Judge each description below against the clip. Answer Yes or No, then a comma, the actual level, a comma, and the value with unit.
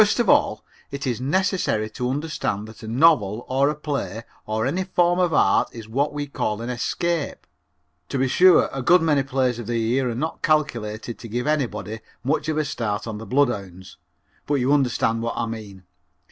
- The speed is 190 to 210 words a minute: Yes, average, 200 wpm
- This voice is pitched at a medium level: No, low, 130 Hz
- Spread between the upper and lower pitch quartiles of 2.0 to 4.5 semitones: No, average, 5.0 semitones